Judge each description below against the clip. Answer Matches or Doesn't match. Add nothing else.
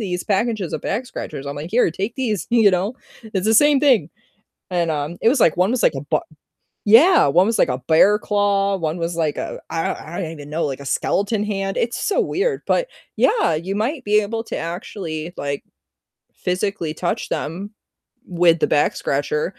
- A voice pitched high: Matches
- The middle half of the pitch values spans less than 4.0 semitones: Doesn't match